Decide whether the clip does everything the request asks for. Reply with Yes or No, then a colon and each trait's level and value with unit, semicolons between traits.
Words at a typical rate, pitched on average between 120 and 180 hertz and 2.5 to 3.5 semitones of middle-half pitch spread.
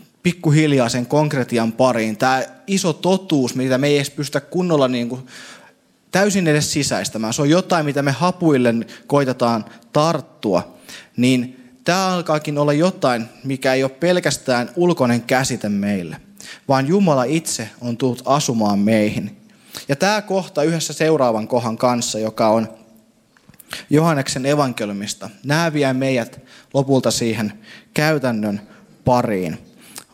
No: average, 125 wpm; low, 130 Hz; average, 4.5 semitones